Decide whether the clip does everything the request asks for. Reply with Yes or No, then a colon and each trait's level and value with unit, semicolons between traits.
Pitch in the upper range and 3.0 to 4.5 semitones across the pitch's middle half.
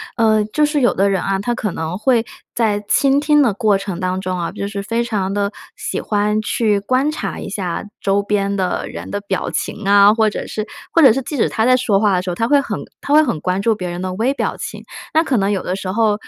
Yes: high, 210 Hz; average, 3.4 semitones